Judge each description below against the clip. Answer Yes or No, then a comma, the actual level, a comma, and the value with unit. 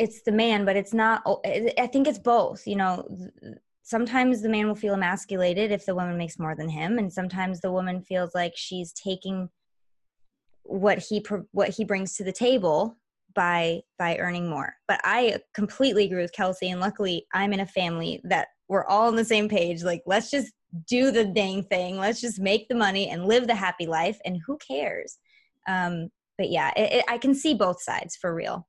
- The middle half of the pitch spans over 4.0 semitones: No, average, 3.6 semitones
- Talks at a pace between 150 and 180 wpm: No, average, 200 wpm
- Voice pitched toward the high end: Yes, high, 195 Hz